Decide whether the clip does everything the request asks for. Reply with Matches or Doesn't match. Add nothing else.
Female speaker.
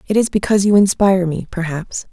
Matches